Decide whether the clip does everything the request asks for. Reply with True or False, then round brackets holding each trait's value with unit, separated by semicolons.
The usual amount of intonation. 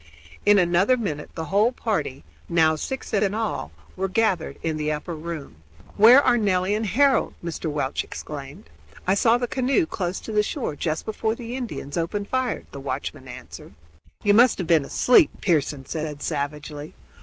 False (6.5 semitones)